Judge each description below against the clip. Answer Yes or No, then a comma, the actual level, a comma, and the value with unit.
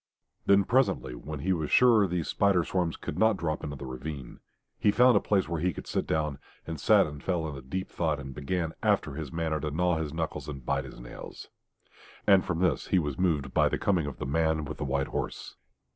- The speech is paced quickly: Yes, fast, 225 wpm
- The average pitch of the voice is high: No, very low, 80 Hz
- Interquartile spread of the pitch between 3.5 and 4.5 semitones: Yes, average, 4.1 semitones